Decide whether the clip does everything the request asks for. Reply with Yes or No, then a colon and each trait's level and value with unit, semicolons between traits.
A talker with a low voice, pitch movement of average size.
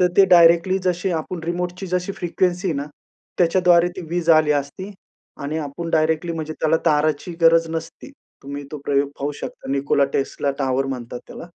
No: medium, 165 Hz; average, 3.6 semitones